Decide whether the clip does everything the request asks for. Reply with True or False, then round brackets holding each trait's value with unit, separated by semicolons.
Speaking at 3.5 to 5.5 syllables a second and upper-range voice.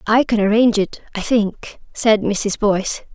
True (4.7 syllables/s; 215 Hz)